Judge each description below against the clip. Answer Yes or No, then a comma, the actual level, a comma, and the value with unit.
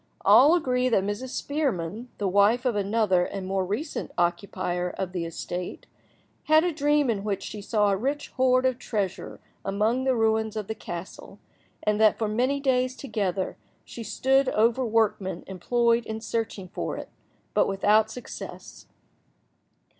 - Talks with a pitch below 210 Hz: No, high, 220 Hz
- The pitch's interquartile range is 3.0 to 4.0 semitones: No, average, 4.4 semitones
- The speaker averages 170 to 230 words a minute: No, average, 155 wpm